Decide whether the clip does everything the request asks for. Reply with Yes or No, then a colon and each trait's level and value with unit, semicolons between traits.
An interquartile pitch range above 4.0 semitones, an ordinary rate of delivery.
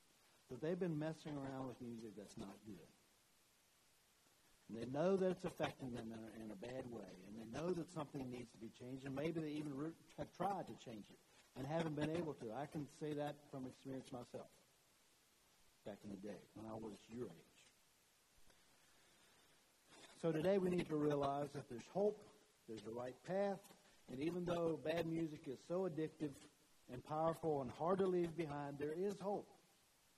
Yes: average, 5.2 semitones; average, 185 wpm